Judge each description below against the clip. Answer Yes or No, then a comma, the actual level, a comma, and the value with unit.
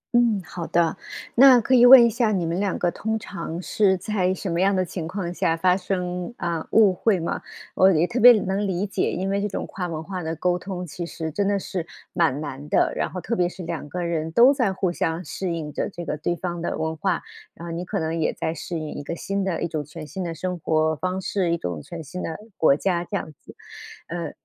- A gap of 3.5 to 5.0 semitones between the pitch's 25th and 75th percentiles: No, average, 3.0 semitones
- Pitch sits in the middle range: Yes, medium, 180 Hz